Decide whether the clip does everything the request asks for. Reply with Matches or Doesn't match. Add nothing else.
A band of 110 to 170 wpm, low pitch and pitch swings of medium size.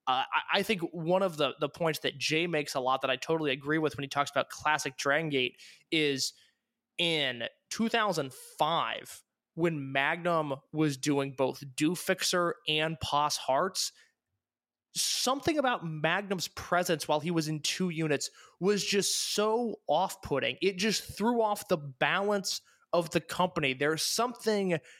Doesn't match